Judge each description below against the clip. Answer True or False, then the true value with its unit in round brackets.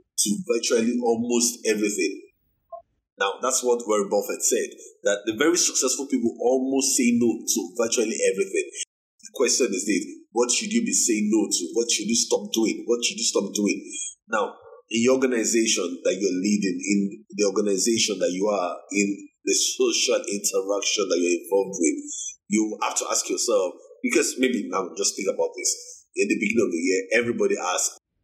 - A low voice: False (305 Hz)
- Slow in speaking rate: False (175 wpm)